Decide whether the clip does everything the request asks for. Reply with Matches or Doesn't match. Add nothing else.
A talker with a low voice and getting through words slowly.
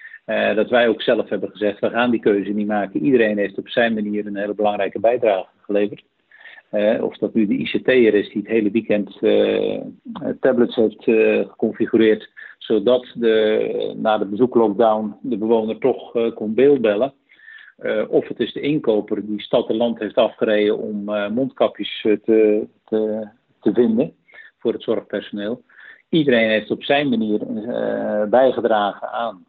Doesn't match